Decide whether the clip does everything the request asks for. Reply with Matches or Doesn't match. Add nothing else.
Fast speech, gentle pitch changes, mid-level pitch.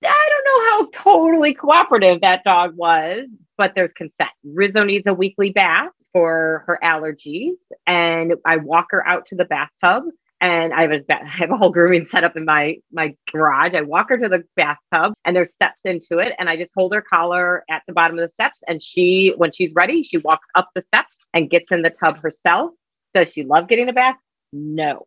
Doesn't match